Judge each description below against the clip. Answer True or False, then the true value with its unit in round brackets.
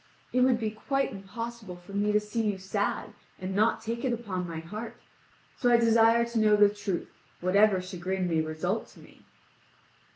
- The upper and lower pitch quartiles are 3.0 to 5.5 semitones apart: True (3.6 semitones)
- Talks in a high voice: True (210 Hz)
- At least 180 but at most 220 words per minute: True (185 wpm)